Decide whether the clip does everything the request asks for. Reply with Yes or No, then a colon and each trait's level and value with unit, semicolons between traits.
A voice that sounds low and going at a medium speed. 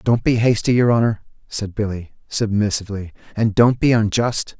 Yes: low, 110 Hz; average, 155 wpm